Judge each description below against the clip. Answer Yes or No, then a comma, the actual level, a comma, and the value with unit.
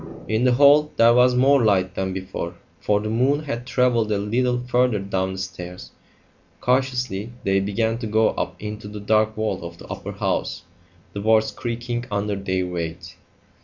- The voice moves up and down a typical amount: Yes, average, 4.1 semitones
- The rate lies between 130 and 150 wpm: No, average, 175 wpm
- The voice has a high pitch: No, low, 110 Hz